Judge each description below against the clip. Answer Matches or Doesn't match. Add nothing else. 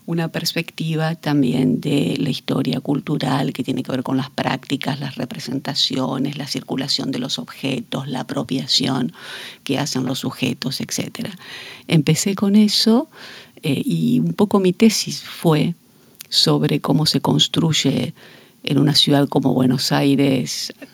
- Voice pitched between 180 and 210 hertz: Doesn't match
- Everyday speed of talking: Matches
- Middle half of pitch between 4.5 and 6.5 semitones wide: Doesn't match